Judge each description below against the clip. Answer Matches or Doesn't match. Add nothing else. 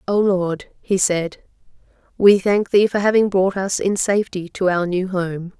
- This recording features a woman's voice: Matches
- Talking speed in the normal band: Matches